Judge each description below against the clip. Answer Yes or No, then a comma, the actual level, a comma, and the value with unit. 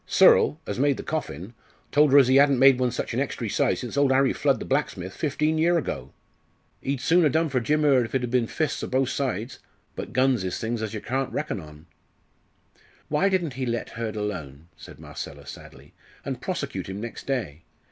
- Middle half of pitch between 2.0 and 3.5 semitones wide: No, average, 4.3 semitones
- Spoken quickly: Yes, fast, 210 wpm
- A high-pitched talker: No, low, 130 Hz